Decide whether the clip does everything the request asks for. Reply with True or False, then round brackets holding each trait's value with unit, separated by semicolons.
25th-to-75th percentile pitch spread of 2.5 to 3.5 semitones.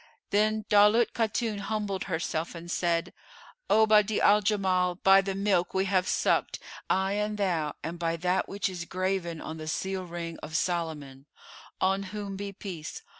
True (3.2 semitones)